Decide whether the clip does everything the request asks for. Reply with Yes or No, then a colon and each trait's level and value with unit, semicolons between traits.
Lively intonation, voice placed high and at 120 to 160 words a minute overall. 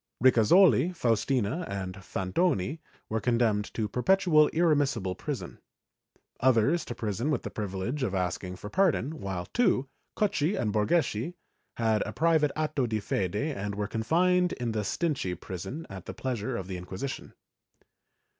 No: wide, 7.2 semitones; low, 120 Hz; average, 145 wpm